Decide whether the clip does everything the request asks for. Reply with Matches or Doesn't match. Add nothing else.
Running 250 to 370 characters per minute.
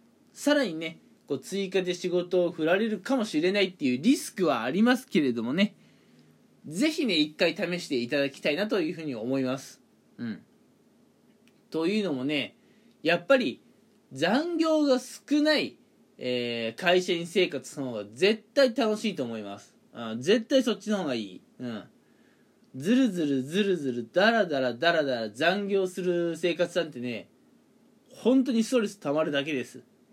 Matches